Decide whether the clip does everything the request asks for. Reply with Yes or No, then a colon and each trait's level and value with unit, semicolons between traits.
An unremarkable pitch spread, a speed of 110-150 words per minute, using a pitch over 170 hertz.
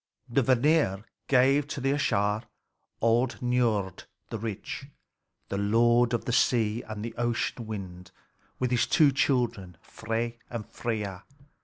No: average, 3.1 semitones; slow, 135 wpm; low, 115 Hz